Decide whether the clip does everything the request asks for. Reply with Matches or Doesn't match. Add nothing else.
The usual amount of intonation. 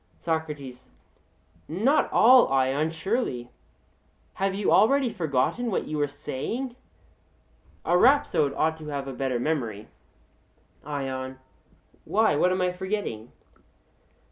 Doesn't match